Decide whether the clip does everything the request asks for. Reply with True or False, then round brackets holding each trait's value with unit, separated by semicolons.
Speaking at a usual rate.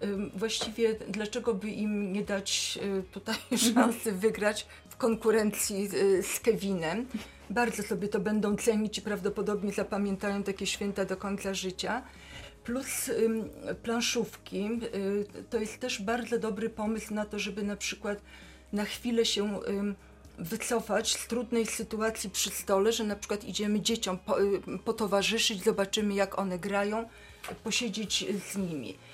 True (125 wpm)